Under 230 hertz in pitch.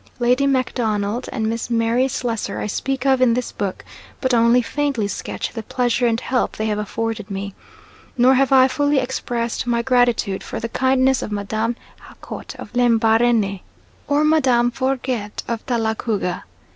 No: high, 240 Hz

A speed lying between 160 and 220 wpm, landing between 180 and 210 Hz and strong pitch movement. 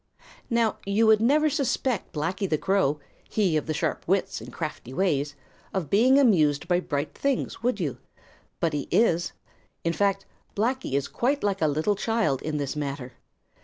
Yes: average, 170 wpm; high, 190 Hz; wide, 7.1 semitones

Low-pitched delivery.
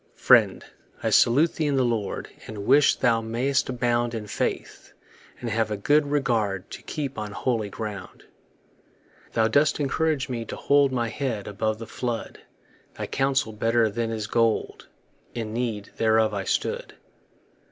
Yes: low, 115 Hz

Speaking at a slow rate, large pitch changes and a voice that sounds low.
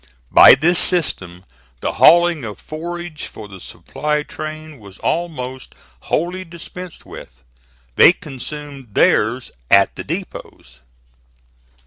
No: slow, 110 wpm; wide, 7.4 semitones; medium, 150 Hz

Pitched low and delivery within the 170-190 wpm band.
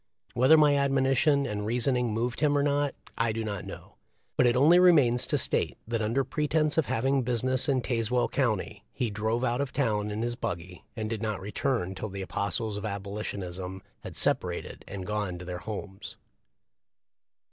Yes: low, 115 Hz; average, 185 wpm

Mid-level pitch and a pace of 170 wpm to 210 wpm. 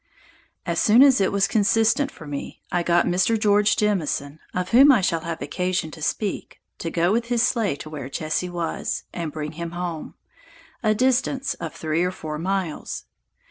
Yes: medium, 180 Hz; average, 180 wpm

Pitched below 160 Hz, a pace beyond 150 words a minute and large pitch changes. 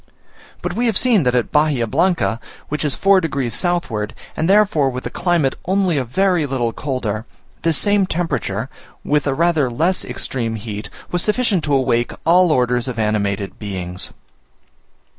Yes: medium, 140 Hz; average, 160 wpm; wide, 7.1 semitones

